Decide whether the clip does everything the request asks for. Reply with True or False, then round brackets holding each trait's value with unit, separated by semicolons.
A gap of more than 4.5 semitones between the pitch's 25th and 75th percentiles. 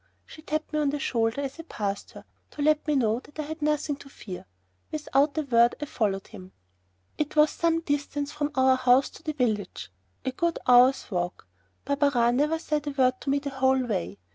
False (3.8 semitones)